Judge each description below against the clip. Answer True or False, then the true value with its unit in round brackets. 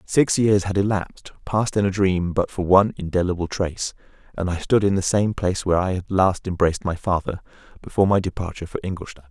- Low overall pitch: True (95 Hz)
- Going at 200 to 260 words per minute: True (205 wpm)